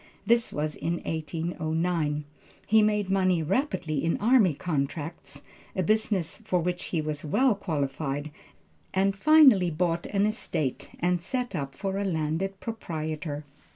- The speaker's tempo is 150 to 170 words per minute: No, slow, 135 wpm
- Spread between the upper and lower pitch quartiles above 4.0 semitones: Yes, average, 4.6 semitones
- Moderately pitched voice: Yes, medium, 175 Hz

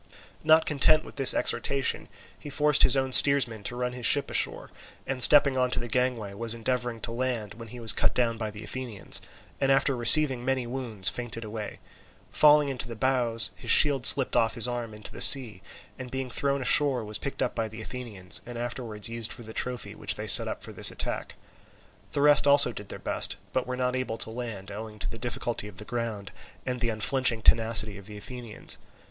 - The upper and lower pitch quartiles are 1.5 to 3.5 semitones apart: Yes, average, 2.9 semitones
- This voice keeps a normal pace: No, fast, 210 wpm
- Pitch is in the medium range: No, low, 120 Hz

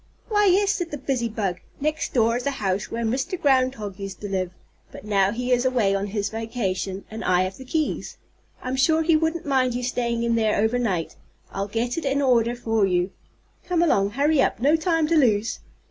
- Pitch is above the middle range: Yes, high, 240 Hz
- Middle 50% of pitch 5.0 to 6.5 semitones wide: Yes, wide, 5.5 semitones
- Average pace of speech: No, fast, 210 wpm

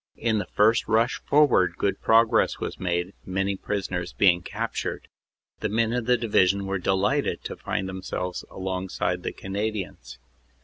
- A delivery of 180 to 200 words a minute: No, average, 160 wpm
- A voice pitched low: Yes, very low, 95 Hz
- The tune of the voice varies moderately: Yes, average, 3.2 semitones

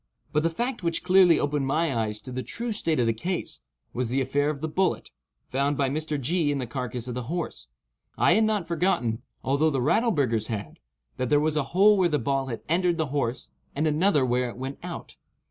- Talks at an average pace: No, fast, 220 wpm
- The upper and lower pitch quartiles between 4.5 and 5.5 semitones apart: Yes, average, 4.8 semitones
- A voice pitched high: No, medium, 145 Hz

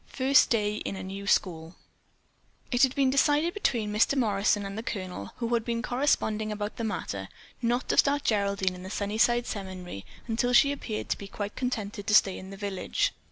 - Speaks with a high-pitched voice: Yes, high, 215 Hz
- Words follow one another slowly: No, average, 195 wpm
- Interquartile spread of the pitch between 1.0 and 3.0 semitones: No, average, 3.7 semitones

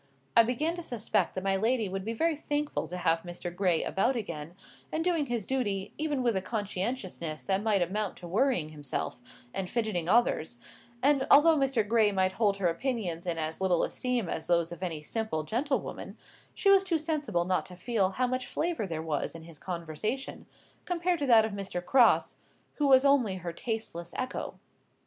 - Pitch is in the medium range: No, high, 210 Hz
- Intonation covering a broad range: Yes, wide, 6.8 semitones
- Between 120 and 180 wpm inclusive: No, average, 190 wpm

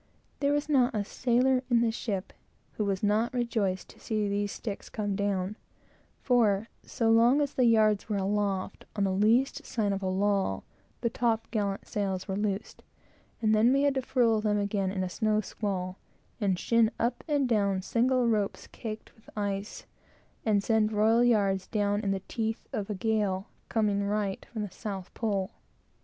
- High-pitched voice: Yes, high, 210 Hz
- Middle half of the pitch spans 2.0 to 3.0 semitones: Yes, narrow, 2.6 semitones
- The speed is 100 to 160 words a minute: No, average, 180 wpm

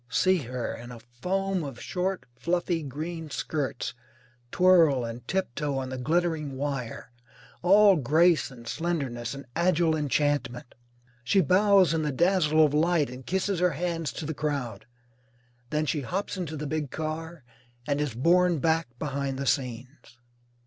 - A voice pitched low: No, medium, 155 Hz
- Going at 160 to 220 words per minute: No, average, 150 wpm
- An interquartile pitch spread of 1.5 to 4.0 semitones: No, average, 4.6 semitones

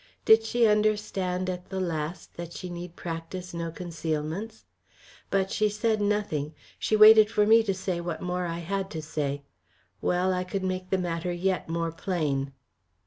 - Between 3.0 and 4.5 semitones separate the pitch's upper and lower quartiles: Yes, average, 3.3 semitones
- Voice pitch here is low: No, medium, 180 Hz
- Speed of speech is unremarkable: Yes, average, 170 wpm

